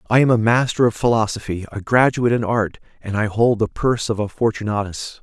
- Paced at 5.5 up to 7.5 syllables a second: Yes, 6.0 syllables/s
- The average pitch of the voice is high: No, low, 110 Hz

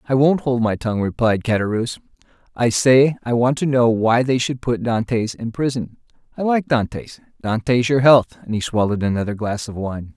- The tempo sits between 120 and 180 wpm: No, average, 195 wpm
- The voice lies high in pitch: No, low, 120 Hz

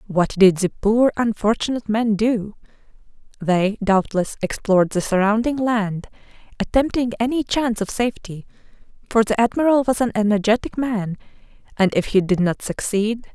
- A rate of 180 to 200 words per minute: No, average, 140 wpm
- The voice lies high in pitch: Yes, high, 215 Hz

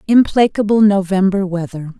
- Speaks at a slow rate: Yes, slow, 90 wpm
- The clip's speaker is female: Yes, female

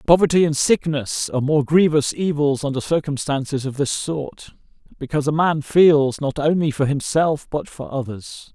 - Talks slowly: No, average, 160 wpm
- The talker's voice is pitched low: No, medium, 145 Hz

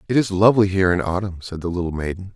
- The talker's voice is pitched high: No, very low, 95 Hz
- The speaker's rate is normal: No, fast, 255 wpm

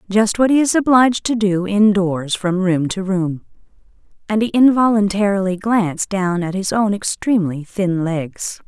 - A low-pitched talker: No, high, 200 Hz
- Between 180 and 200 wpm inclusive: No, average, 160 wpm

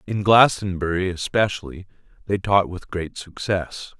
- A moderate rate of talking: No, slow, 120 wpm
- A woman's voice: No, male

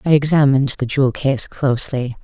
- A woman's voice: Yes, female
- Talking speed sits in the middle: Yes, average, 160 wpm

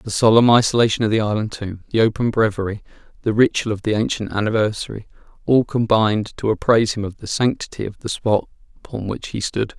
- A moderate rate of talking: Yes, average, 190 wpm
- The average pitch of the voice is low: Yes, low, 110 Hz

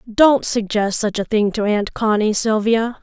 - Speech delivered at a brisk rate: No, average, 180 wpm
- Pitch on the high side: Yes, high, 220 Hz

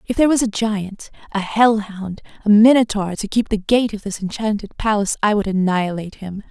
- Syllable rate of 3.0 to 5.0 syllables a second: No, 5.6 syllables/s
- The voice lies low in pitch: No, high, 210 Hz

